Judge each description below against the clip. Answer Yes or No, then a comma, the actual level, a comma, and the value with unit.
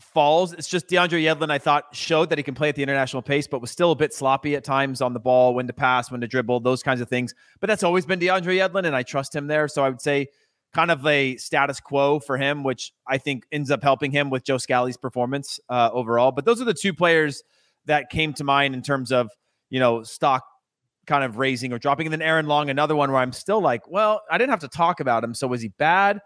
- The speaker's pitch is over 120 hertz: Yes, medium, 140 Hz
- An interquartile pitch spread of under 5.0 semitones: Yes, average, 3.5 semitones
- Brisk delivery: Yes, fast, 265 wpm